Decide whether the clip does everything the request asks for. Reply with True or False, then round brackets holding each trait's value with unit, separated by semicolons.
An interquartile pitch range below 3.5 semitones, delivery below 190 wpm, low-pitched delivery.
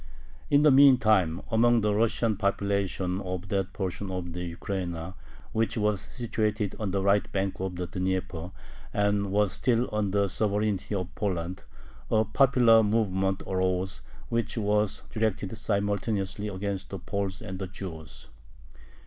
True (2.4 semitones; 140 wpm; 100 Hz)